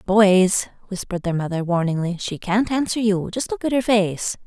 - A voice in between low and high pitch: No, high, 200 Hz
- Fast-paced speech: No, average, 190 wpm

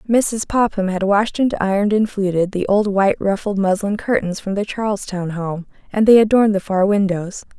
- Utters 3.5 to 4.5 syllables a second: No, 5.4 syllables/s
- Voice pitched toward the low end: No, high, 200 Hz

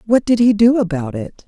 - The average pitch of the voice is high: Yes, high, 205 Hz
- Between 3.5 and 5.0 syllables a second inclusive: No, 5.3 syllables/s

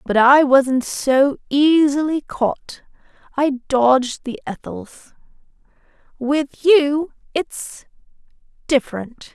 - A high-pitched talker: Yes, very high, 275 Hz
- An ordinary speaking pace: No, slow, 90 wpm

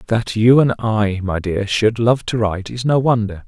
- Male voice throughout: Yes, male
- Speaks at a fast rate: Yes, fast, 225 wpm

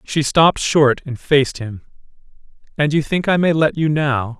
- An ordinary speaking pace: Yes, average, 190 wpm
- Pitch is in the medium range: Yes, medium, 145 Hz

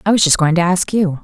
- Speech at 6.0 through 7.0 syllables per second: Yes, 6.3 syllables/s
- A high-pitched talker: No, medium, 180 Hz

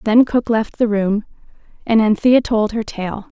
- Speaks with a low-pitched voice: No, high, 220 Hz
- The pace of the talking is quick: No, average, 175 wpm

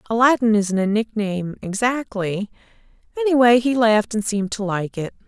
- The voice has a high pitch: Yes, high, 220 Hz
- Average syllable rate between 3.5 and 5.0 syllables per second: No, 5.5 syllables/s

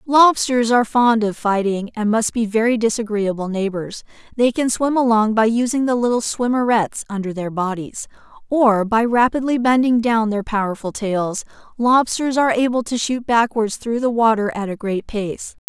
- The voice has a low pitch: No, high, 225 Hz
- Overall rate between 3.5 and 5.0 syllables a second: Yes, 4.8 syllables/s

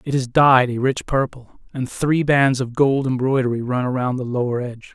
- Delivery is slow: No, fast, 205 wpm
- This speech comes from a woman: No, male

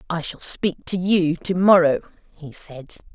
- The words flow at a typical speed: Yes, average, 155 wpm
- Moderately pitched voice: Yes, medium, 170 Hz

